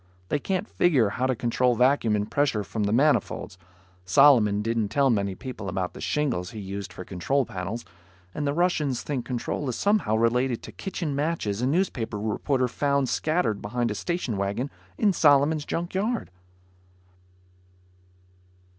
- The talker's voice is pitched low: Yes, low, 125 Hz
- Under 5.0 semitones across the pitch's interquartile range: No, wide, 5.6 semitones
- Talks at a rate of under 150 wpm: No, average, 155 wpm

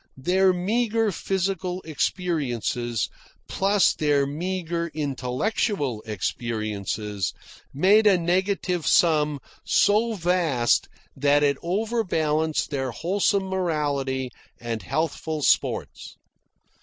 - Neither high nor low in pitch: Yes, medium, 160 Hz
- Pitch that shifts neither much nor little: No, wide, 5.8 semitones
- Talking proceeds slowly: Yes, slow, 85 wpm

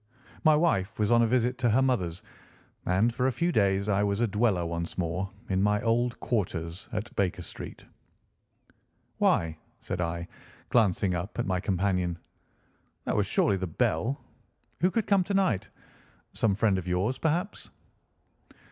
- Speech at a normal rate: Yes, average, 160 wpm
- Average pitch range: Yes, average, 4.7 semitones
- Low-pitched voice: Yes, low, 105 Hz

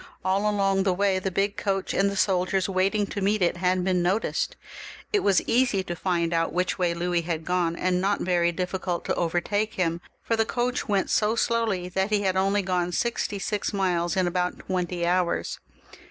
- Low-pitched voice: No, high, 190 Hz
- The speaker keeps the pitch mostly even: Yes, narrow, 2.2 semitones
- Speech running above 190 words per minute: Yes, average, 200 wpm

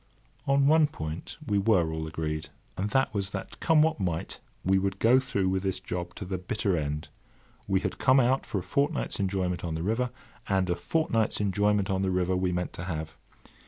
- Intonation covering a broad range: No, average, 3.8 semitones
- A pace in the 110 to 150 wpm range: No, fast, 205 wpm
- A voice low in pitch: Yes, very low, 95 Hz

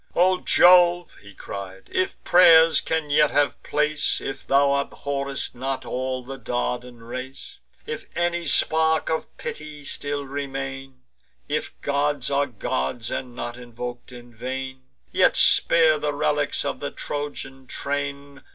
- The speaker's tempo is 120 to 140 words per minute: Yes, slow, 135 wpm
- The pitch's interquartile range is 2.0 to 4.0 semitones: Yes, average, 2.8 semitones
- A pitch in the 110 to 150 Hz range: Yes, medium, 140 Hz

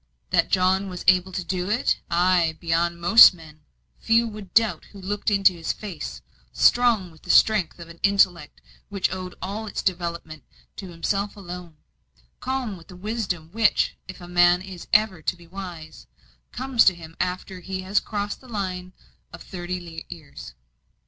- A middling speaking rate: Yes, average, 170 wpm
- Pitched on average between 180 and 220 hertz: Yes, medium, 185 Hz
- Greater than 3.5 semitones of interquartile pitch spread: No, average, 2.8 semitones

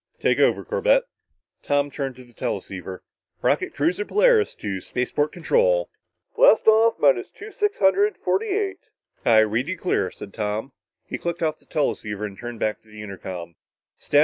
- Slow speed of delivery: No, average, 170 wpm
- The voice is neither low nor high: Yes, medium, 145 Hz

